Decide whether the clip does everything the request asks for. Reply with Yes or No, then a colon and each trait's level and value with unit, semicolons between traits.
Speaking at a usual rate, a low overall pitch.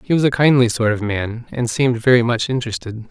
No: fast, 230 wpm; low, 120 Hz